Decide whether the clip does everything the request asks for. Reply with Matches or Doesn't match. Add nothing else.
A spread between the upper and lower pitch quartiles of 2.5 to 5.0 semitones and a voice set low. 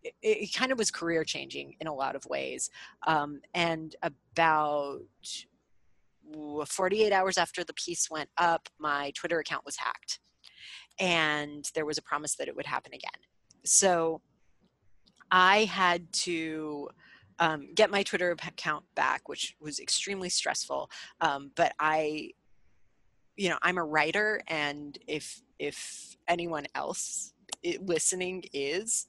Doesn't match